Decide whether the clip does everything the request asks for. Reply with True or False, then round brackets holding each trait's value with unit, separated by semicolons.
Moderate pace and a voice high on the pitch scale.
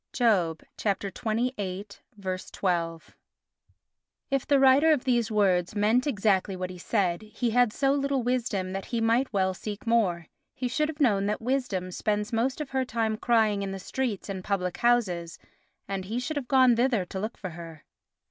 True (175 wpm; 215 Hz)